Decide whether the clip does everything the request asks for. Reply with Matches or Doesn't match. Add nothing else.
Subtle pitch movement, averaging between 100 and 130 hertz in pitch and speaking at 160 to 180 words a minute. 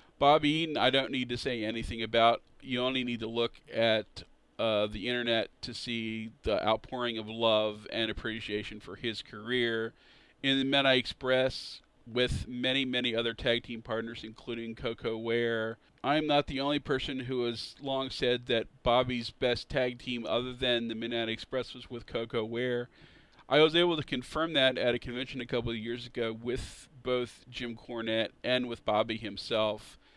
Matches